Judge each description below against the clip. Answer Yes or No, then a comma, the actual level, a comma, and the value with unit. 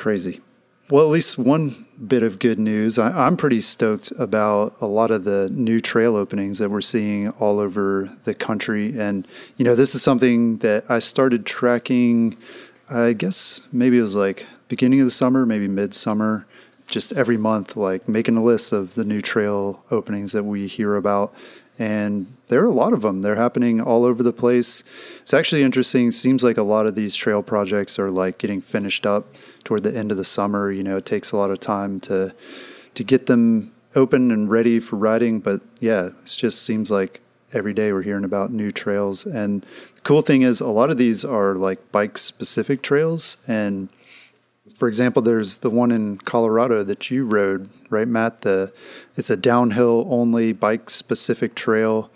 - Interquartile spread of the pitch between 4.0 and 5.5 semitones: No, average, 3.0 semitones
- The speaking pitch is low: Yes, low, 110 Hz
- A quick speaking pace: No, average, 190 wpm